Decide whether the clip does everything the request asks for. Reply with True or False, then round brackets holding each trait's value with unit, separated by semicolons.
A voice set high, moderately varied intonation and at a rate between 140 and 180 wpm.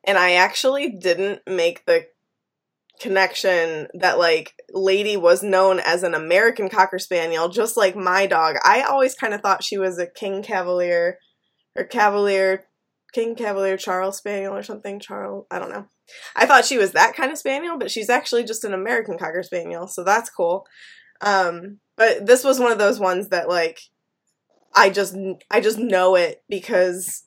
True (195 Hz; 3.7 semitones; 175 wpm)